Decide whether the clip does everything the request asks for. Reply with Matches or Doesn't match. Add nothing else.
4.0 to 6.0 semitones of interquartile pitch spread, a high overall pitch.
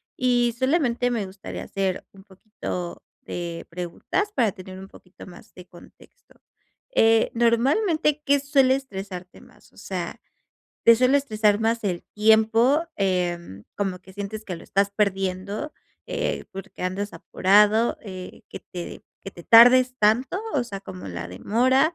Matches